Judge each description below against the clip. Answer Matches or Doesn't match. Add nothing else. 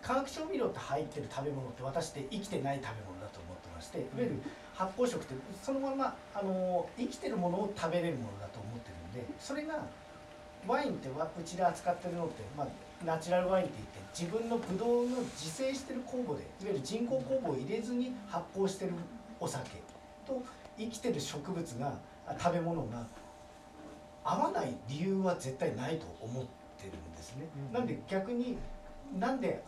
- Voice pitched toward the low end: Doesn't match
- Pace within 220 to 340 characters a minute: Doesn't match